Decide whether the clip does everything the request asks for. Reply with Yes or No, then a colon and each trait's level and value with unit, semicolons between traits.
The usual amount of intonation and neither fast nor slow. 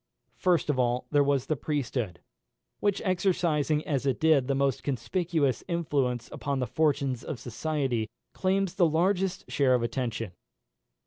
Yes: average, 4.7 semitones; average, 145 wpm